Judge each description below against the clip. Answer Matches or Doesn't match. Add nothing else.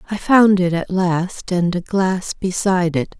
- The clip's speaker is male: Doesn't match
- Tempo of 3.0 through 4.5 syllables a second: Matches